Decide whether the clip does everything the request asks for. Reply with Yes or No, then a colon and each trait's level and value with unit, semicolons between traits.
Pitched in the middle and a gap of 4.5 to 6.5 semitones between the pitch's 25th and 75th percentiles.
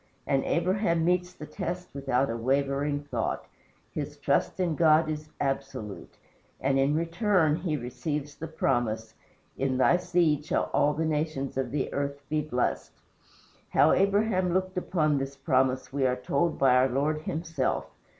No: medium, 150 Hz; average, 3.7 semitones